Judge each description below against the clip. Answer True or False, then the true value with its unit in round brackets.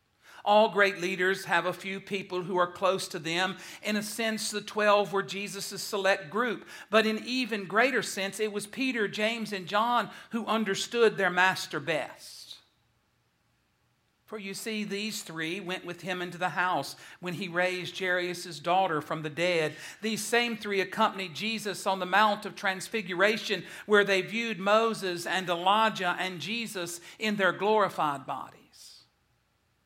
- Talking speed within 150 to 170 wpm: True (155 wpm)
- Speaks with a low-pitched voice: False (195 Hz)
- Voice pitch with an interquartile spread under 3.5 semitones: True (2.9 semitones)